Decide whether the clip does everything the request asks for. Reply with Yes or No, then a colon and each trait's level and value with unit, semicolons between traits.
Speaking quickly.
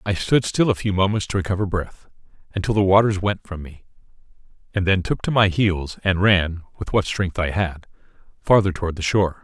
Yes: fast, 210 wpm